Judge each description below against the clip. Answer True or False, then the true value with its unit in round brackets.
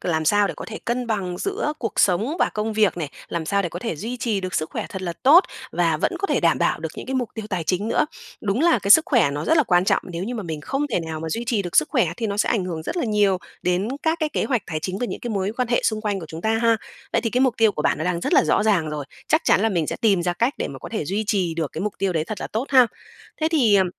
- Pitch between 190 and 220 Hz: True (205 Hz)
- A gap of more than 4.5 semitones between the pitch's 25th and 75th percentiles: True (5.2 semitones)